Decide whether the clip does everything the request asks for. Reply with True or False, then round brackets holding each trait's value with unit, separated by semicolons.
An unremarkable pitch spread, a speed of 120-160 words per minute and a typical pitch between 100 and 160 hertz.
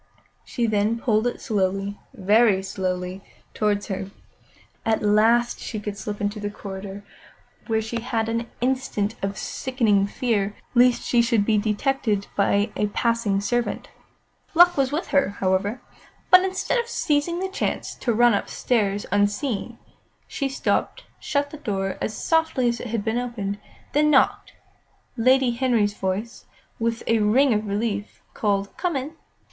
False (3.7 semitones; 150 wpm; 225 Hz)